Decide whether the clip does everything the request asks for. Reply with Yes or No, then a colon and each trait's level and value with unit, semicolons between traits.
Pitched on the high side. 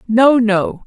Yes: high, 225 Hz